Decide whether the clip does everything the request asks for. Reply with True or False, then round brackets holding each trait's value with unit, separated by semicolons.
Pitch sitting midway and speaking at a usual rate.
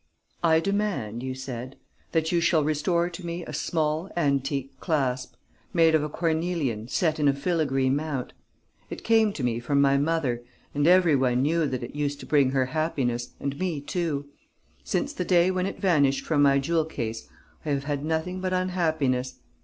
True (150 Hz; 185 wpm)